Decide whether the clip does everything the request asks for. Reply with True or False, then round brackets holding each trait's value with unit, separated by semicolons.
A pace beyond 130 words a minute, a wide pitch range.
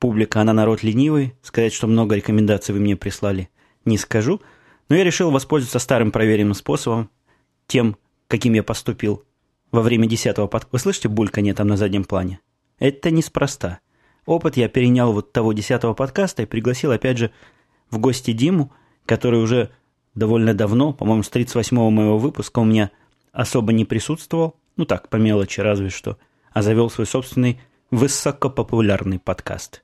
False (155 wpm; 3.3 semitones)